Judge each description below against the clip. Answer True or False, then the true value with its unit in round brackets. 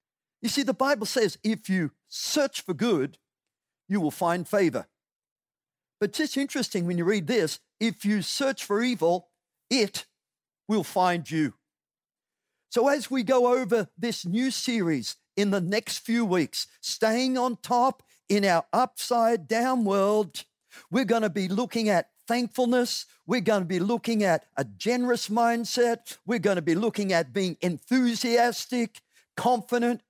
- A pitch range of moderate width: True (3.9 semitones)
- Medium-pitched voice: False (225 Hz)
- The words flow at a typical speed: True (155 wpm)